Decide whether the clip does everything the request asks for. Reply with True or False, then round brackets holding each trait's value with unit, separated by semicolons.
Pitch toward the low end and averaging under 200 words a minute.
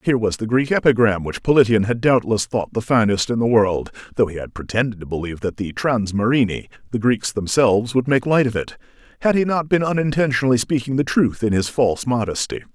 False (115 Hz; 205 wpm)